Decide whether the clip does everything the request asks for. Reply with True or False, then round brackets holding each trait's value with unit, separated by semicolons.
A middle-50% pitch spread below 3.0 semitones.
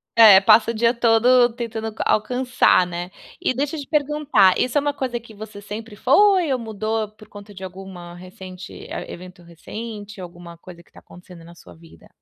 False (4.7 semitones)